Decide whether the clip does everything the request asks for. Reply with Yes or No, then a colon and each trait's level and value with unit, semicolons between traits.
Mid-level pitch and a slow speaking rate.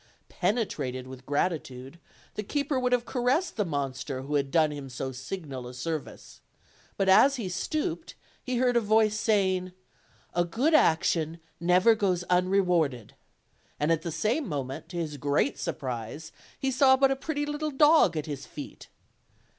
No: medium, 180 Hz; average, 160 wpm